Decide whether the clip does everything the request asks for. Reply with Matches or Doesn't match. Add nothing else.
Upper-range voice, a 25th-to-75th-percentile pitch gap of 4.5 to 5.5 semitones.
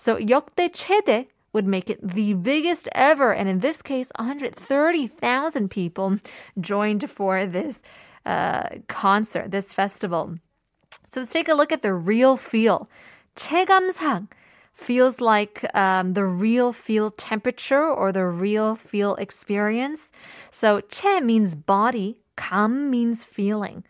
Matches